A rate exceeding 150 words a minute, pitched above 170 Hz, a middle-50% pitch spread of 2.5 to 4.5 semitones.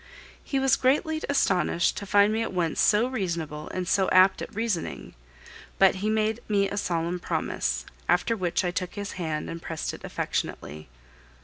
Yes: average, 175 wpm; high, 190 Hz; average, 4.2 semitones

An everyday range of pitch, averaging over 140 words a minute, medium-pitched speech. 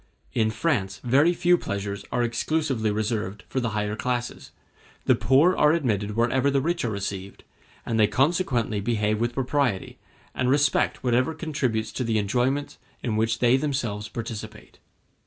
No: average, 4.2 semitones; average, 155 wpm; low, 120 Hz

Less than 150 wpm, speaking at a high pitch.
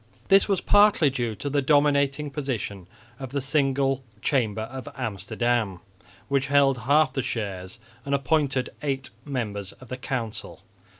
No: average, 140 wpm; low, 135 Hz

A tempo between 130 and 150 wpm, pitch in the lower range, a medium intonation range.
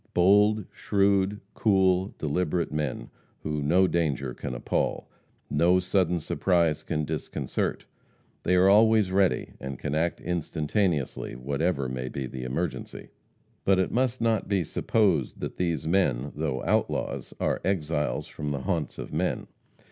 Yes: average, 140 wpm; very low, 85 Hz; average, 4.7 semitones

